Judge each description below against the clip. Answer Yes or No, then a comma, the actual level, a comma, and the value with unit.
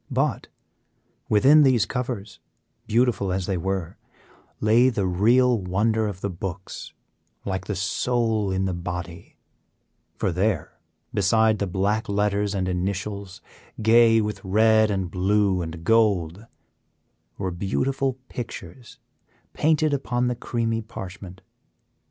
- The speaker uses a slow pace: Yes, slow, 120 wpm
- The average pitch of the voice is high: No, low, 100 Hz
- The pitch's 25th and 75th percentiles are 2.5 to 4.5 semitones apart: Yes, average, 3.3 semitones